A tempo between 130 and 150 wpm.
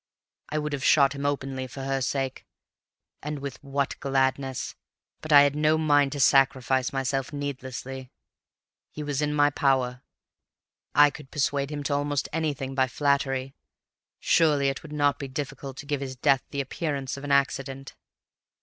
No: average, 165 wpm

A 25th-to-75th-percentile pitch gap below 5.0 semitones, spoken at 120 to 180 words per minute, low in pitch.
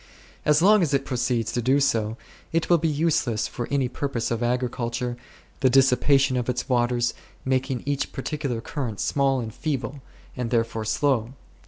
Yes: average, 2.9 semitones; average, 160 wpm; low, 125 Hz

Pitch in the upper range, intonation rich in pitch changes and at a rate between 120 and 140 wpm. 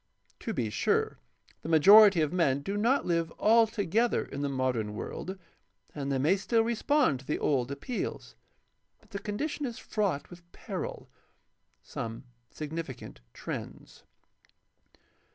No: medium, 170 Hz; wide, 7.5 semitones; slow, 135 wpm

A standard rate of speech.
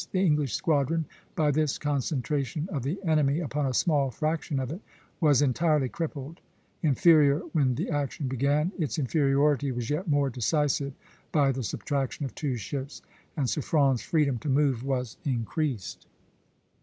Yes: average, 150 wpm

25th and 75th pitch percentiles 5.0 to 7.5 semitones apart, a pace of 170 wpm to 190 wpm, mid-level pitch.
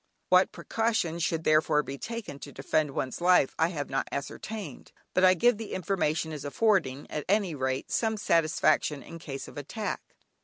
Yes: average, 5.3 semitones; average, 175 wpm; medium, 160 Hz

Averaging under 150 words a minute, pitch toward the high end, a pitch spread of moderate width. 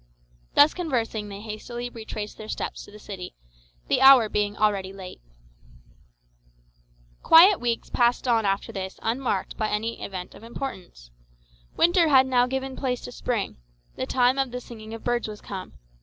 No: average, 160 wpm; high, 230 Hz; average, 3.6 semitones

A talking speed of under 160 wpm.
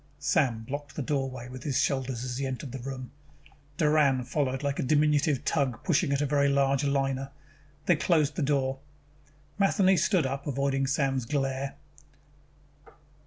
Yes: average, 150 wpm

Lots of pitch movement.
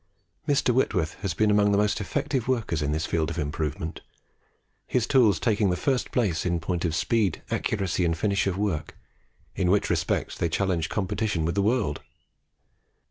No: average, 4.6 semitones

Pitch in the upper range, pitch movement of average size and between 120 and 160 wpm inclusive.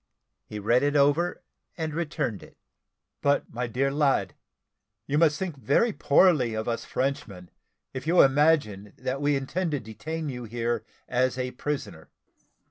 No: low, 135 Hz; average, 3.9 semitones; average, 150 wpm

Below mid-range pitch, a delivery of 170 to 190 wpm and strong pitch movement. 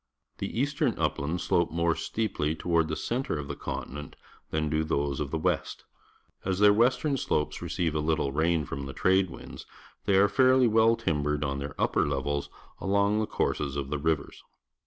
Yes: very low, 80 Hz; average, 180 wpm; wide, 5.8 semitones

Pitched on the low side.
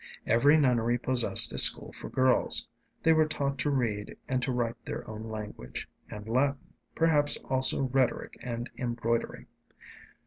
Yes: low, 125 Hz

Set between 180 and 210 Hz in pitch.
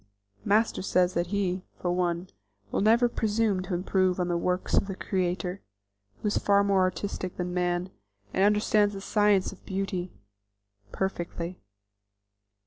Yes: high, 190 Hz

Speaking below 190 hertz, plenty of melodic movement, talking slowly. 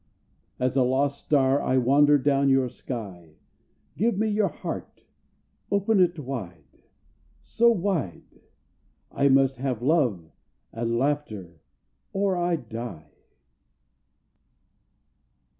Yes: low, 135 Hz; wide, 6.1 semitones; slow, 105 wpm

